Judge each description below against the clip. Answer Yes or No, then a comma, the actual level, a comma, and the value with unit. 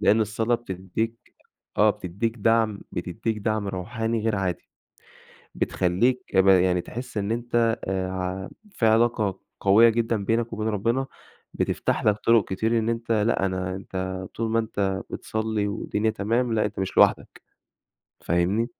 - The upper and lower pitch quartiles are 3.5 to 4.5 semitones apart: No, average, 3.1 semitones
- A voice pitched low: Yes, low, 110 Hz